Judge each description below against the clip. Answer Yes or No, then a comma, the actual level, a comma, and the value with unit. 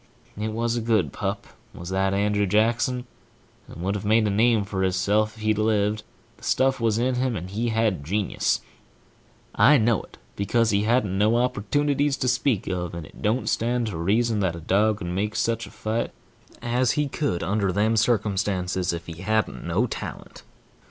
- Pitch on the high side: No, low, 110 Hz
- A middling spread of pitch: Yes, average, 3.3 semitones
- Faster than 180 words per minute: Yes, average, 190 wpm